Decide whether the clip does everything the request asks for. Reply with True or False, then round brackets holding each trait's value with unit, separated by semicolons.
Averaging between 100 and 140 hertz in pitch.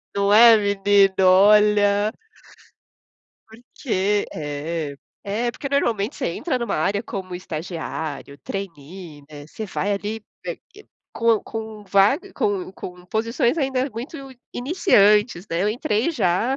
False (205 Hz)